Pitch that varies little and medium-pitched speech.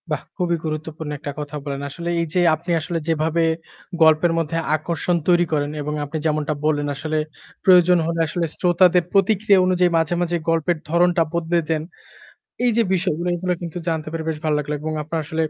Yes: narrow, 2.2 semitones; medium, 165 Hz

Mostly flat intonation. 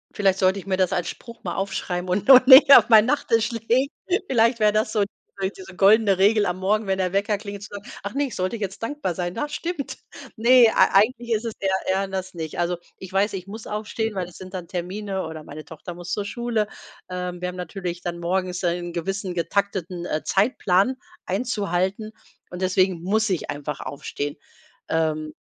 No: average, 3.3 semitones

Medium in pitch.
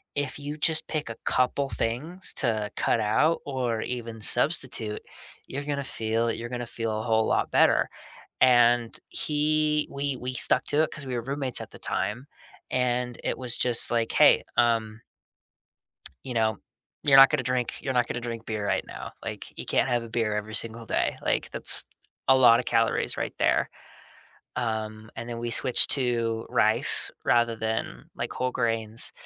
No: low, 120 Hz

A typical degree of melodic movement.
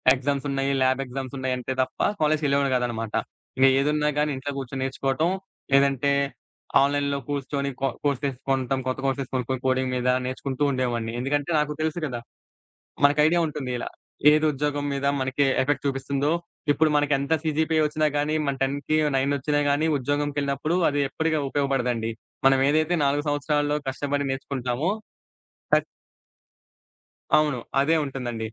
No: narrow, 1.9 semitones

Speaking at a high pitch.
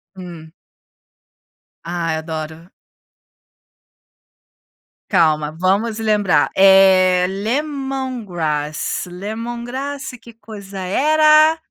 Yes: high, 195 Hz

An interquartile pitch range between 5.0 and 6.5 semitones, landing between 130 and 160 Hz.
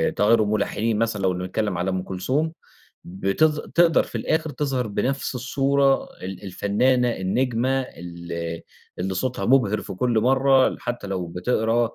No: wide, 5.6 semitones; low, 115 Hz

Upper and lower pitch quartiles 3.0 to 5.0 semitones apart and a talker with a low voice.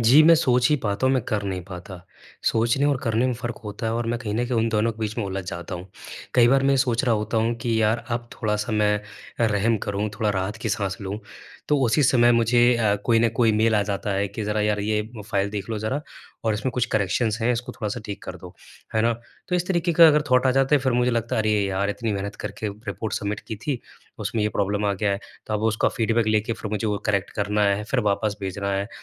No: narrow, 2.6 semitones; low, 110 Hz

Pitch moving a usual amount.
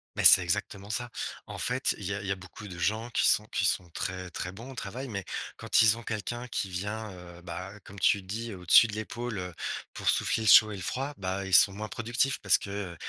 Yes: average, 3.6 semitones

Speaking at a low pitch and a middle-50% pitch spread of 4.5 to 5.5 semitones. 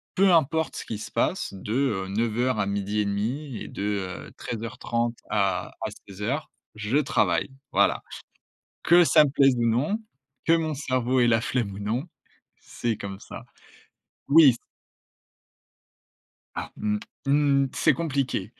Yes: low, 120 Hz; average, 5.1 semitones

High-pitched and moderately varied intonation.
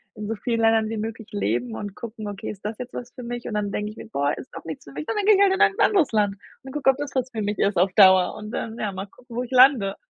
Yes: high, 220 Hz; average, 3.9 semitones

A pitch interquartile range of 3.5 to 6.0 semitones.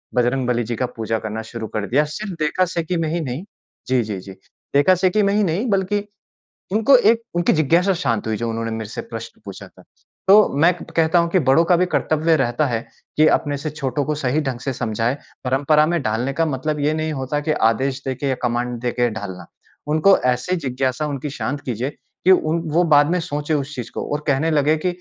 Yes: average, 5.1 semitones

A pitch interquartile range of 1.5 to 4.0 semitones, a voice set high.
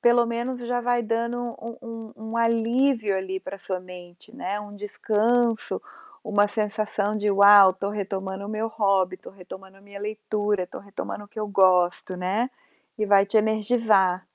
Yes: average, 2.8 semitones; high, 210 Hz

